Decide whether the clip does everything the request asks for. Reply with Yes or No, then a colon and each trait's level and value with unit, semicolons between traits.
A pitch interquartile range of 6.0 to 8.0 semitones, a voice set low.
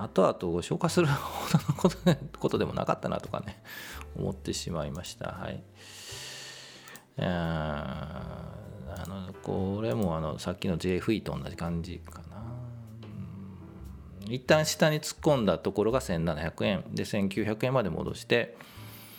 Yes: wide, 6.3 semitones; low, 100 Hz